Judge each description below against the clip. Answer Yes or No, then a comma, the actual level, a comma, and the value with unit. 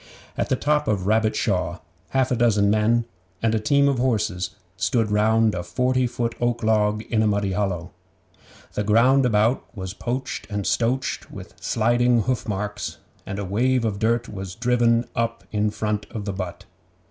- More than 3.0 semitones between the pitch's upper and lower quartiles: No, average, 2.7 semitones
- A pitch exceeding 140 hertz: No, low, 110 Hz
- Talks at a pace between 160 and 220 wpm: Yes, average, 170 wpm